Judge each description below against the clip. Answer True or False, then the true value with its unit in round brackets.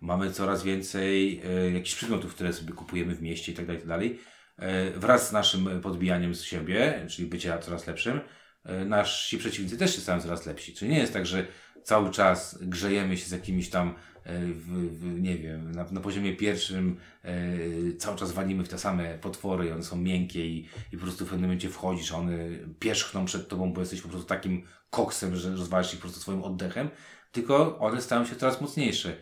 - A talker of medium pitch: False (90 Hz)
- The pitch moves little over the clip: True (1.9 semitones)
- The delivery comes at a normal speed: False (200 wpm)